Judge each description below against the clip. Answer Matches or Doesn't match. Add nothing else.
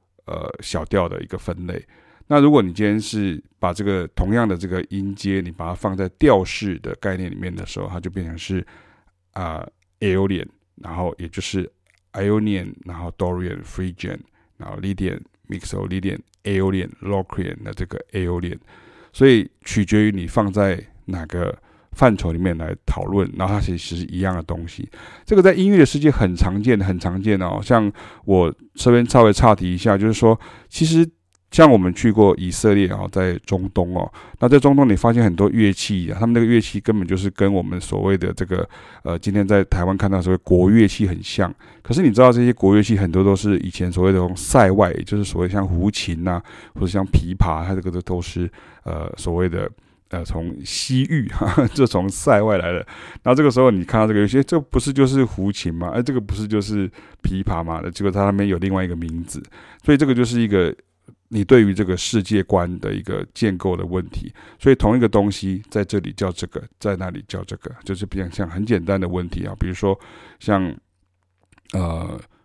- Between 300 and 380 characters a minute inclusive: Matches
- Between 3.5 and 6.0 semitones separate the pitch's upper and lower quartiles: Doesn't match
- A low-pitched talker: Matches